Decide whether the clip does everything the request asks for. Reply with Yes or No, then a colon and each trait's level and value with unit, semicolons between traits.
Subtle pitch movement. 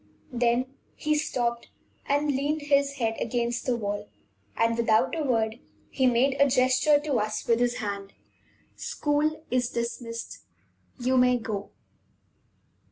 No: average, 3.3 semitones